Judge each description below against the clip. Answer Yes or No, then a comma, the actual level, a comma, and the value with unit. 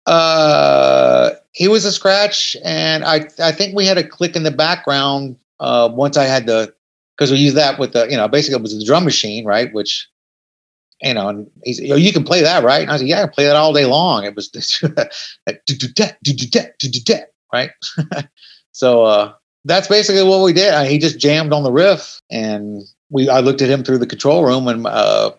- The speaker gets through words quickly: Yes, fast, 210 wpm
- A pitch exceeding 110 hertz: Yes, medium, 140 Hz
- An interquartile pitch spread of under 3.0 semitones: No, average, 4.6 semitones